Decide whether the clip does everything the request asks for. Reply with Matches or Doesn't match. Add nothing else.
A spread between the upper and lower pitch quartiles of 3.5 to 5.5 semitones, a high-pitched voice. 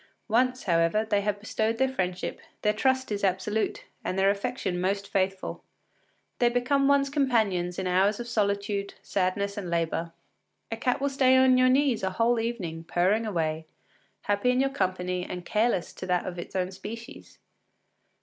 Matches